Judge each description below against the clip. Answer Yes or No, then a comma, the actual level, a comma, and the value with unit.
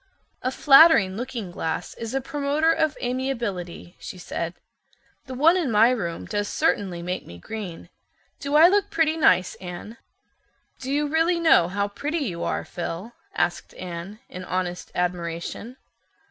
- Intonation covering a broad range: Yes, wide, 8.1 semitones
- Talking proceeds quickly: No, average, 150 wpm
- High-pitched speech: Yes, high, 220 Hz